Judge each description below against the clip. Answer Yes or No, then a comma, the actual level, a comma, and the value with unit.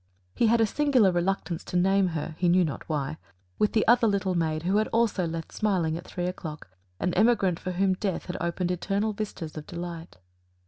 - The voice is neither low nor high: Yes, medium, 180 Hz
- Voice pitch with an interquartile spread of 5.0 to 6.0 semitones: No, average, 3.4 semitones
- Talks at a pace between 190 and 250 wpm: Yes, average, 200 wpm